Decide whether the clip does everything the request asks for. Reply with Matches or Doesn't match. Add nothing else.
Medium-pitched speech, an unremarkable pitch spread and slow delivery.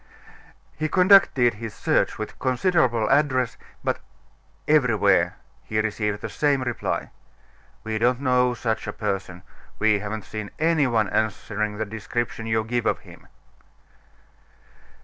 Doesn't match